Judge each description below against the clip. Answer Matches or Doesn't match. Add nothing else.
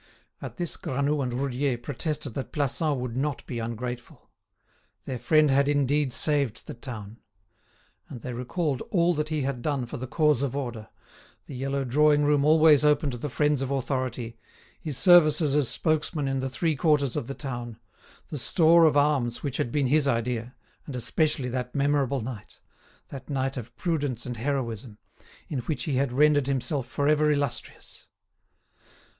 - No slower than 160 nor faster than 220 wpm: Matches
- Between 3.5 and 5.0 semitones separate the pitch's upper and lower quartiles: Doesn't match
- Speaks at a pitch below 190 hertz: Matches